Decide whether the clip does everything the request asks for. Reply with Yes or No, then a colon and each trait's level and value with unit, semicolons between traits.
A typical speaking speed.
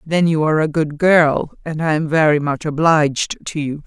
No: fast, 215 wpm